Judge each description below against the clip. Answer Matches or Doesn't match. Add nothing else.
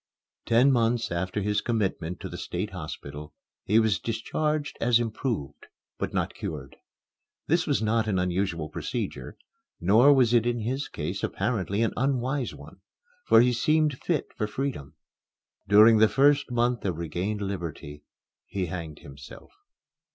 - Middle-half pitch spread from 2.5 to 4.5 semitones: Doesn't match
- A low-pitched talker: Matches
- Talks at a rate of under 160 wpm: Matches